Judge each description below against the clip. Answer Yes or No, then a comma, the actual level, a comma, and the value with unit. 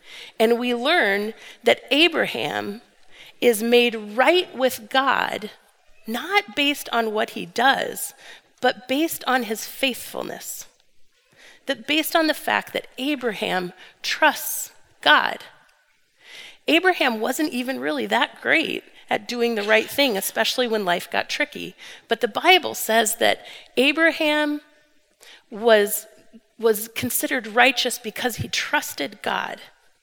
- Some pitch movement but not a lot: Yes, average, 4.9 semitones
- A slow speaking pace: Yes, slow, 120 wpm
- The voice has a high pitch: Yes, very high, 255 Hz